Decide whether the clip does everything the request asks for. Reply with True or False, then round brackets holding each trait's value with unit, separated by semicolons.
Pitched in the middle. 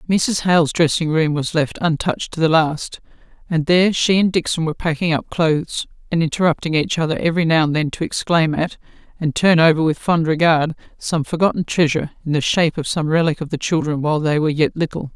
True (160 Hz)